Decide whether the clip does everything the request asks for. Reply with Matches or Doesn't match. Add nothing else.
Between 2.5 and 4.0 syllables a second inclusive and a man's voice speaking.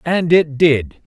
Matches